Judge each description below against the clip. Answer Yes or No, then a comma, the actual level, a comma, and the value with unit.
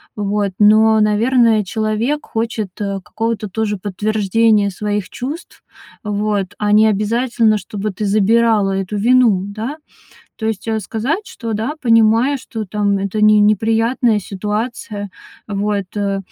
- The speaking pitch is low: No, high, 215 Hz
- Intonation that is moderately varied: No, narrow, 1.8 semitones